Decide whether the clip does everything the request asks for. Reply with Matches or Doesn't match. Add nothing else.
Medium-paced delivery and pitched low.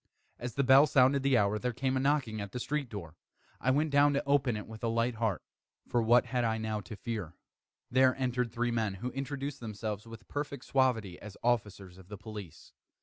Doesn't match